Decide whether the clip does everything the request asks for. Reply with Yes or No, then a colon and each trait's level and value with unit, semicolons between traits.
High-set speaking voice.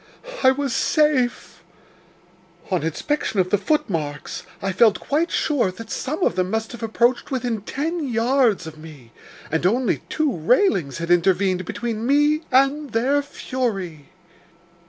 Yes: high, 230 Hz